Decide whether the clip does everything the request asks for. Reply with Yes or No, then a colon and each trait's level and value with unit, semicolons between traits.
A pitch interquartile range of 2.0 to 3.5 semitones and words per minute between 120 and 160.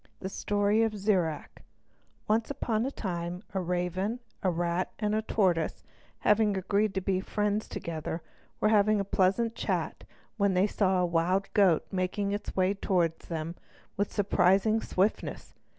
Yes: average, 2.7 semitones; average, 150 wpm